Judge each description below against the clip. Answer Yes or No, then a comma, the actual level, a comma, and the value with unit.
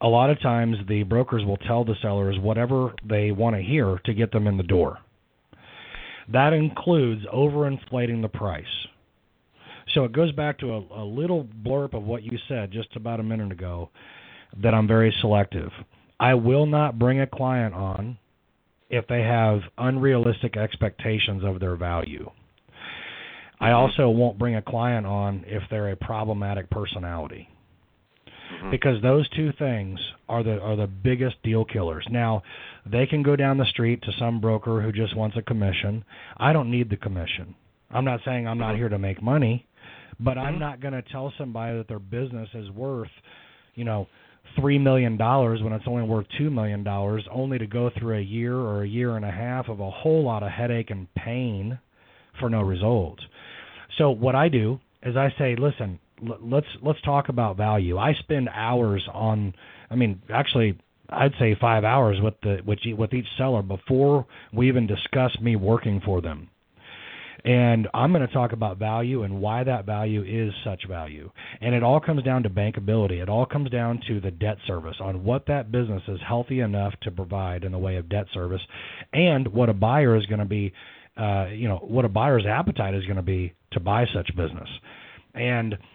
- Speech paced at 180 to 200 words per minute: Yes, average, 185 wpm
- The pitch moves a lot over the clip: No, average, 3.6 semitones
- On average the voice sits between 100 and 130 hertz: Yes, low, 115 Hz